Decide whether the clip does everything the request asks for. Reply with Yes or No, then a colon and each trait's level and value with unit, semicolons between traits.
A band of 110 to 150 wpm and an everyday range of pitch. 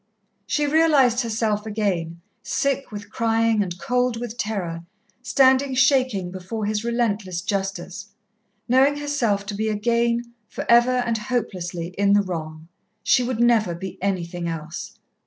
Yes: average, 140 wpm; average, 4.4 semitones